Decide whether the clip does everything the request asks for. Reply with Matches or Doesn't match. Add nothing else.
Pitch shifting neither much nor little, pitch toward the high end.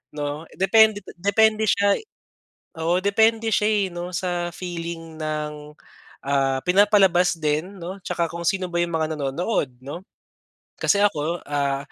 Doesn't match